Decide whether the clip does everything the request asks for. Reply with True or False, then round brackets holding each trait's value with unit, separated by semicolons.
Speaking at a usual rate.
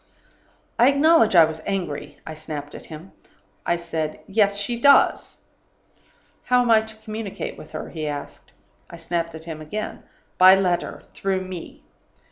True (155 wpm)